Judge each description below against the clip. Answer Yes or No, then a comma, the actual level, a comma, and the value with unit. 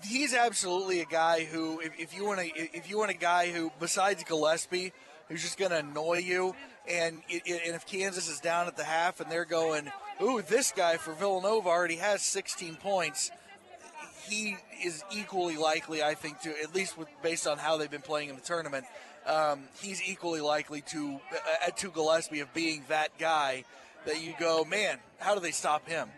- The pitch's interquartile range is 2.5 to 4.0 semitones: Yes, average, 3.2 semitones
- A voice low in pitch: No, medium, 170 Hz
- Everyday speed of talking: Yes, average, 195 wpm